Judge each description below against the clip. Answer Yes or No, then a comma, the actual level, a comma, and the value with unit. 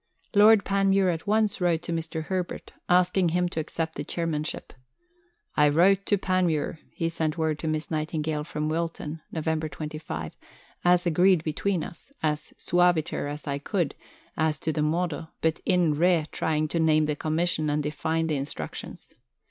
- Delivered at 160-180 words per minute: Yes, average, 165 wpm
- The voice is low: No, medium, 160 Hz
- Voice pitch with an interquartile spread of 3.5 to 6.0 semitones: No, narrow, 2.6 semitones